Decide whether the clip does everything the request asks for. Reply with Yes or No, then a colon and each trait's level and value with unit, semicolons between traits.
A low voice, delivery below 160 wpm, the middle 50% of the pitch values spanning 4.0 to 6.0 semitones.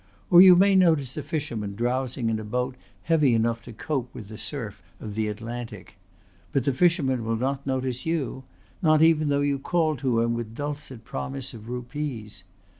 No: low, 130 Hz; average, 185 wpm; average, 4.3 semitones